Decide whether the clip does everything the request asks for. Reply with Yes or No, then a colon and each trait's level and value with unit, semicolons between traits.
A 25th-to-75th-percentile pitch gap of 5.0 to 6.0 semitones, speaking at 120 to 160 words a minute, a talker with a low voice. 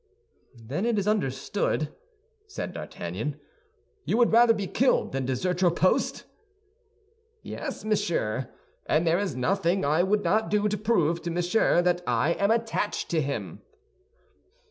No: wide, 5.4 semitones; average, 145 wpm; medium, 180 Hz